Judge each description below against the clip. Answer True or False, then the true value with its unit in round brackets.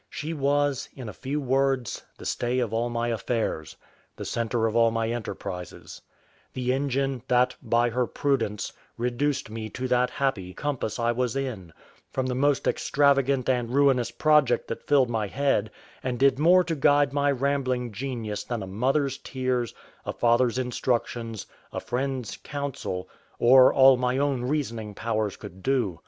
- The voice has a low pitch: True (125 Hz)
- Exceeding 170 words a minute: False (160 wpm)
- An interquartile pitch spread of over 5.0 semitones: False (3.0 semitones)